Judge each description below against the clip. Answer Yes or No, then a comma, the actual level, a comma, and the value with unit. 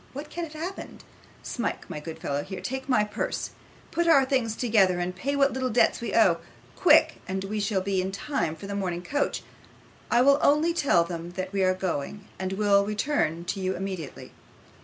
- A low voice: No, high, 200 Hz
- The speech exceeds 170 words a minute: Yes, average, 200 wpm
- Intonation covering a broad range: Yes, wide, 6.6 semitones